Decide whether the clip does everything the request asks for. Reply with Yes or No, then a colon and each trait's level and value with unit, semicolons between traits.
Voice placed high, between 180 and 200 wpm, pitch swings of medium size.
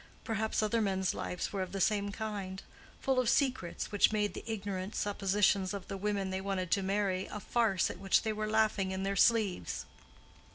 No: high, 200 Hz; average, 190 wpm; narrow, 2.0 semitones